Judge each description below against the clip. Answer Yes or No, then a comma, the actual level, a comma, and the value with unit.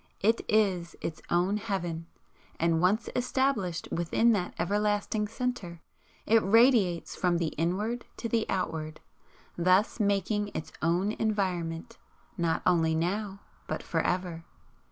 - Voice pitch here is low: No, high, 190 Hz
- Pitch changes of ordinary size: Yes, average, 4.0 semitones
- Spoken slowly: Yes, slow, 125 wpm